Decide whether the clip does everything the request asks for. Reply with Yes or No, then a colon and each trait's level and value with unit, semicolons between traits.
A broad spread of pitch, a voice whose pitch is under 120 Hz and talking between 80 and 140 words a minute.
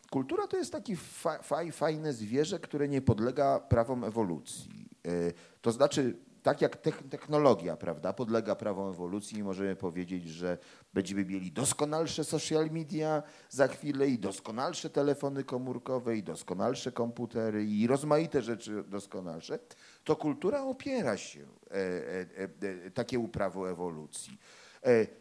No: wide, 7.3 semitones; low, 125 Hz; average, 115 wpm